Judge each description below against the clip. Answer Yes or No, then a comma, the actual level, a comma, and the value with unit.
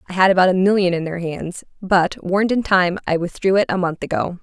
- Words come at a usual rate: No, fast, 245 wpm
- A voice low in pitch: No, medium, 185 Hz